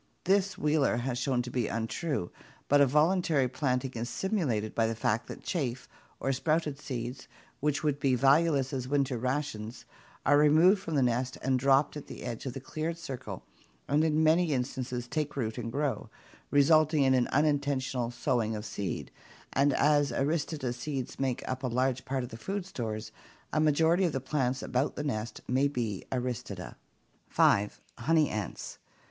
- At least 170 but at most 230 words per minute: Yes, average, 175 wpm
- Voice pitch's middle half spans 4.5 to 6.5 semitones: No, average, 3.6 semitones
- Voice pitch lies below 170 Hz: Yes, low, 135 Hz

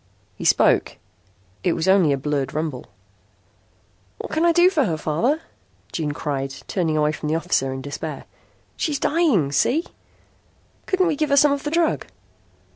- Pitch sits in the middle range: Yes, medium, 170 Hz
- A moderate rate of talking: Yes, average, 165 wpm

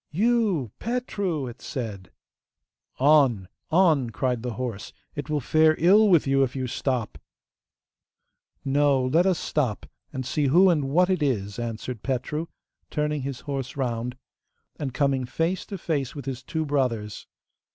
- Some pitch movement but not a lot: Yes, average, 4.1 semitones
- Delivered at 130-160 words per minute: Yes, average, 150 wpm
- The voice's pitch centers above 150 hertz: No, medium, 140 Hz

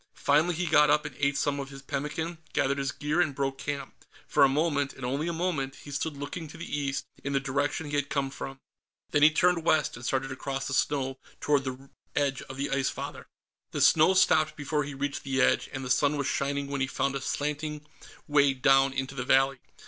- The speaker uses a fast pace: Yes, fast, 225 wpm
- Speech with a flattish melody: Yes, narrow, 1.7 semitones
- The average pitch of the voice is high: No, medium, 140 Hz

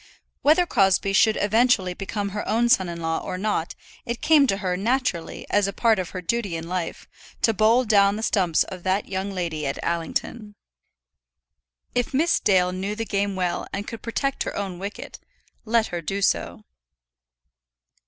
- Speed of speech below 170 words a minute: No, average, 175 wpm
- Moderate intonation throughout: Yes, average, 3.6 semitones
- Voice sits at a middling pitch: No, high, 200 Hz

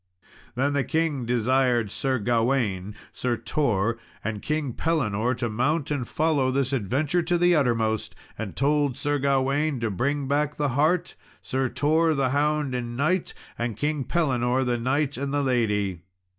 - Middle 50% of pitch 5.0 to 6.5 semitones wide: No, average, 3.8 semitones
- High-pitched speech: No, low, 135 Hz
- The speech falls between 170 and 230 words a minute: No, average, 155 wpm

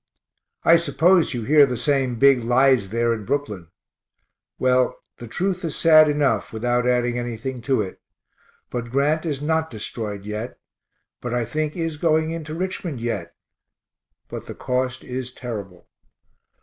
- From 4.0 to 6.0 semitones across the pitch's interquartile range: Yes, average, 4.6 semitones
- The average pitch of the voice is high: No, low, 130 Hz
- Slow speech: No, average, 150 wpm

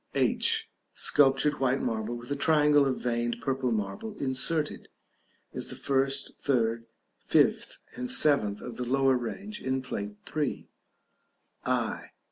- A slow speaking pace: Yes, slow, 130 wpm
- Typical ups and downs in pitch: Yes, average, 3.4 semitones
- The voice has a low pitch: Yes, low, 130 Hz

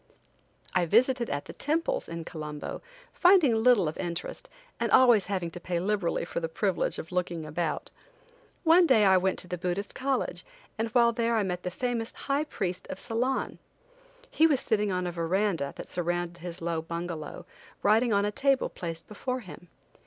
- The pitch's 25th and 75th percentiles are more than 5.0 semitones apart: Yes, wide, 5.6 semitones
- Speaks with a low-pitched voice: No, high, 190 Hz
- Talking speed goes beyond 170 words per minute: Yes, average, 180 wpm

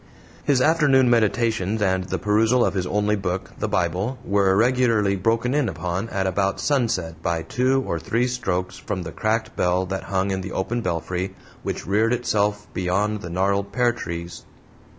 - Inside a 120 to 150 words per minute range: No, average, 170 wpm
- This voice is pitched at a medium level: No, low, 100 Hz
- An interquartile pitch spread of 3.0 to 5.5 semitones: Yes, average, 4.0 semitones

